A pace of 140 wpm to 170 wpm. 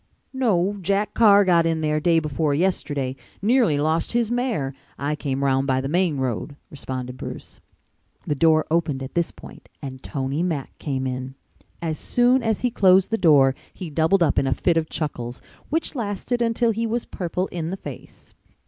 No: average, 185 wpm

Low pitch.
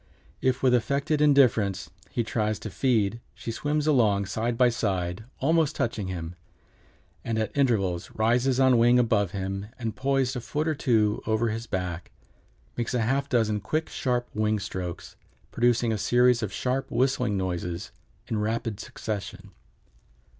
Yes: low, 115 Hz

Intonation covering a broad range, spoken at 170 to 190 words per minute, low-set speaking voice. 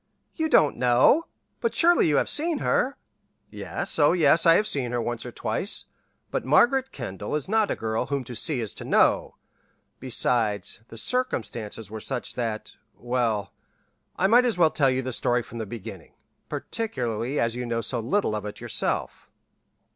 Yes: wide, 8.0 semitones; average, 175 wpm; low, 125 Hz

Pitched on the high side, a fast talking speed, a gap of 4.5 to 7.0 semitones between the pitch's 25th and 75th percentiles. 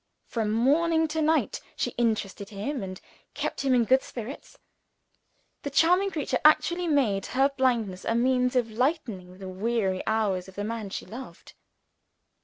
No: high, 240 Hz; average, 155 wpm; wide, 5.4 semitones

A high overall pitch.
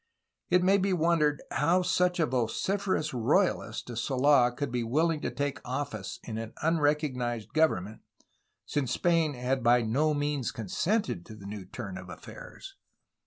No: medium, 140 Hz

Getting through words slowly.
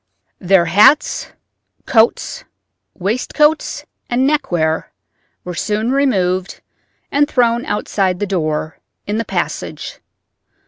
Yes: slow, 95 wpm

